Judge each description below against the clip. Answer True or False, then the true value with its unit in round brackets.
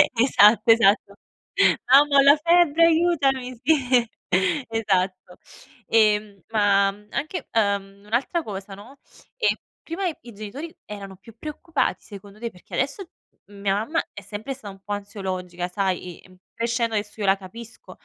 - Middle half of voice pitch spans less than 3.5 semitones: False (5.3 semitones)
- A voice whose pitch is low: False (215 Hz)